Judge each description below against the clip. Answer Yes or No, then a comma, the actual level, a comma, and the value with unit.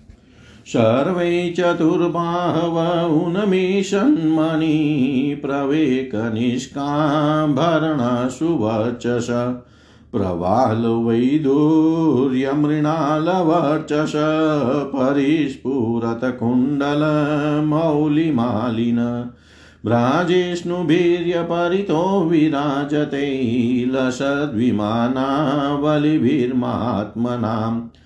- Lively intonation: No, average, 4.5 semitones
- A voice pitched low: No, medium, 145 Hz